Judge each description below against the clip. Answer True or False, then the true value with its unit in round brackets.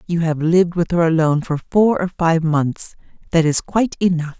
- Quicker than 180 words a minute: True (205 wpm)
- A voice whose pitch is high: False (170 Hz)